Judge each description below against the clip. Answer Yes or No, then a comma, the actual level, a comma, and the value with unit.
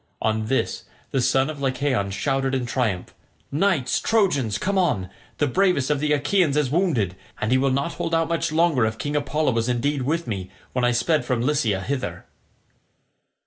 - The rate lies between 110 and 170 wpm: No, average, 185 wpm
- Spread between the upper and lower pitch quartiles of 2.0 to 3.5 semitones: No, average, 4.1 semitones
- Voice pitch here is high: No, low, 135 Hz